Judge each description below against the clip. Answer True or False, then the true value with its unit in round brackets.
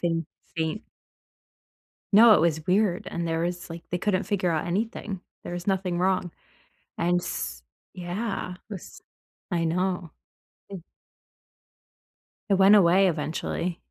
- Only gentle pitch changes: True (2.3 semitones)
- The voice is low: False (180 Hz)